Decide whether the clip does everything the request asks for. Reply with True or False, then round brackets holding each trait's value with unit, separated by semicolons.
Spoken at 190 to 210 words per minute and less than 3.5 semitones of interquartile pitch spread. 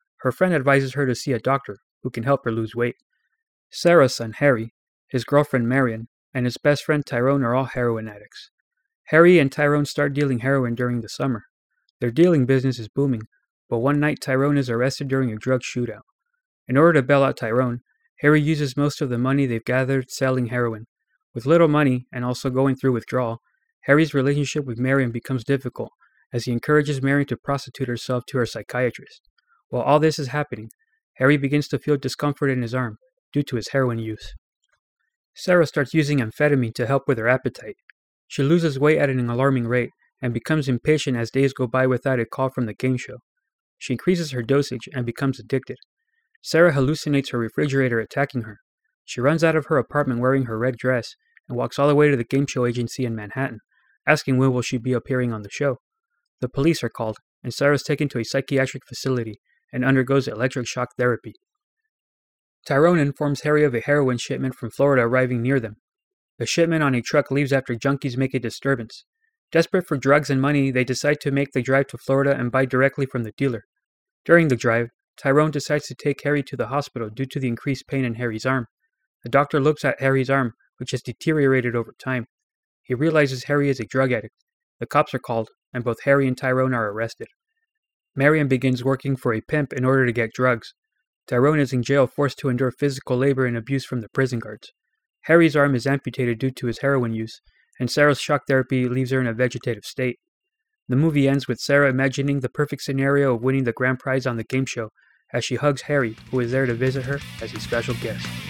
True (205 wpm; 2.7 semitones)